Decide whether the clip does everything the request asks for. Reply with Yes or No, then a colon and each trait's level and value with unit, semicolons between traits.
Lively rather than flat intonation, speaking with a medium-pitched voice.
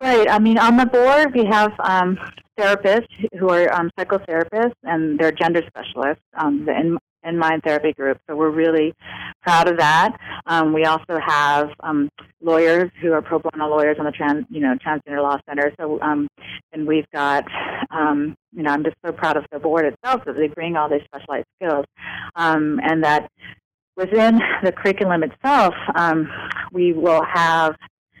No: average, 3.4 semitones; medium, 160 Hz